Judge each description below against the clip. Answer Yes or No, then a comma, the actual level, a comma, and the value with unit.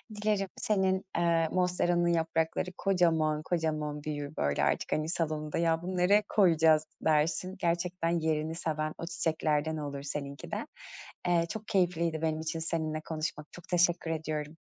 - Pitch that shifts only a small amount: Yes, narrow, 2.2 semitones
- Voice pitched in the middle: Yes, medium, 165 Hz